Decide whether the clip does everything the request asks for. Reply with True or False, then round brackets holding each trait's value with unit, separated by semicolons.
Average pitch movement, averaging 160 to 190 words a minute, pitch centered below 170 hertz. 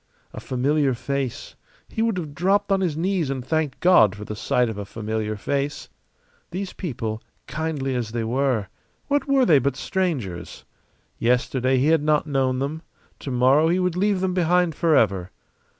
False (6.0 semitones; 170 wpm; 140 Hz)